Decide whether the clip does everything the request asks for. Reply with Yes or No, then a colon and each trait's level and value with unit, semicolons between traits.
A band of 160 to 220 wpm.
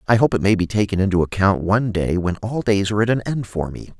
No: fast, 285 wpm